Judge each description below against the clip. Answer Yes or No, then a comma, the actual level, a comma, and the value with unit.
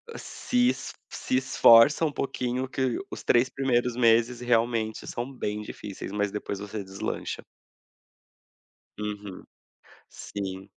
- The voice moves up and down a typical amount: Yes, average, 3.6 semitones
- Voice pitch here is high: No, low, 115 Hz